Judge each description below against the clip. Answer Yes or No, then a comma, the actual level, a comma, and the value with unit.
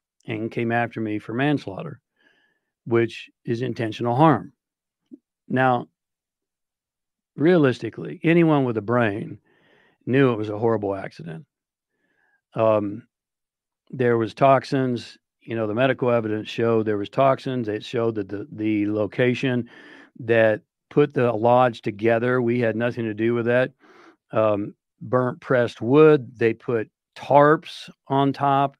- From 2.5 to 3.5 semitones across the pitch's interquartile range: Yes, average, 2.9 semitones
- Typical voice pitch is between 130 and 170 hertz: No, low, 120 Hz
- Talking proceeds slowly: Yes, slow, 130 wpm